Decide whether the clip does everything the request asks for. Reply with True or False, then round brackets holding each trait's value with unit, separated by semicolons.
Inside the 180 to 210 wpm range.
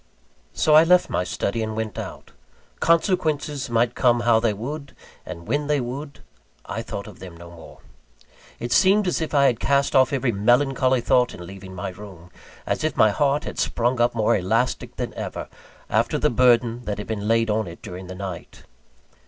True (195 wpm)